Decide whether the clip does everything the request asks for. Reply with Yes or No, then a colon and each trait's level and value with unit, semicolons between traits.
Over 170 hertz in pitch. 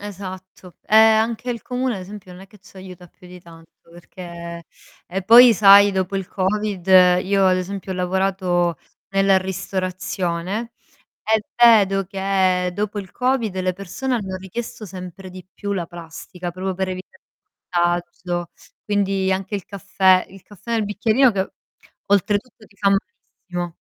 Yes: high, 190 Hz